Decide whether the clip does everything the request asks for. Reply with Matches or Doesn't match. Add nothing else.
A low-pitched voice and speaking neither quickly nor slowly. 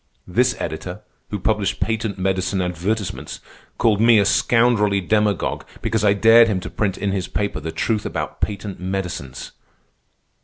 Matches